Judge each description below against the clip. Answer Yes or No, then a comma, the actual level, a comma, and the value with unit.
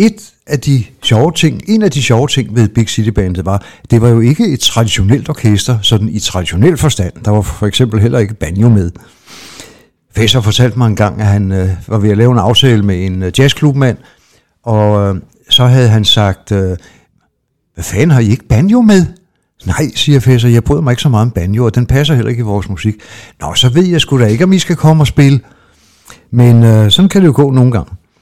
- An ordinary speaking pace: No, fast, 230 wpm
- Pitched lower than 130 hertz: Yes, low, 115 Hz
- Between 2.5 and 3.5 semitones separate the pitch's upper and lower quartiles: No, average, 4.7 semitones